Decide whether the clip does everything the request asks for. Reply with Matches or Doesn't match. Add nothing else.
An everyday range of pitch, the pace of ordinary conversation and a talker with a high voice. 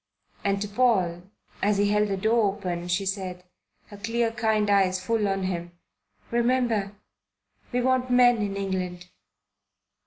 Matches